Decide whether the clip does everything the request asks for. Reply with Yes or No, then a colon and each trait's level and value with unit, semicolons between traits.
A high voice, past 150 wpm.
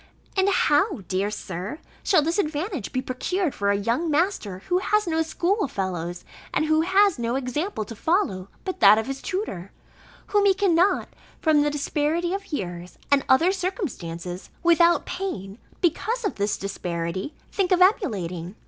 Yes: very high, 295 Hz; average, 160 wpm